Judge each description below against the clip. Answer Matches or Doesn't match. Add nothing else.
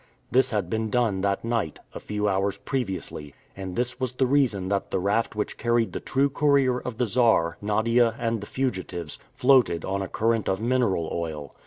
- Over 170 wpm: Matches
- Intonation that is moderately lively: Matches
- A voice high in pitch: Doesn't match